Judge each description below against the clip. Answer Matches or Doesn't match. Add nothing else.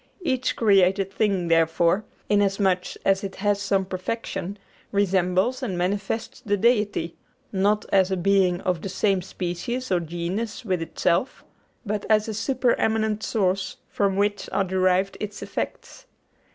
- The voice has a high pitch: Matches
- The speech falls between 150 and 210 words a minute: Doesn't match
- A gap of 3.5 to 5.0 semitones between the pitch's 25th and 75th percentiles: Doesn't match